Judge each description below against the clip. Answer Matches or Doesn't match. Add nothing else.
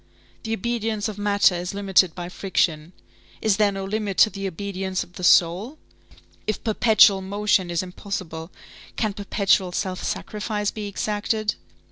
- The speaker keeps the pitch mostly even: Matches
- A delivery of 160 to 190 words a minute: Doesn't match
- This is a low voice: Doesn't match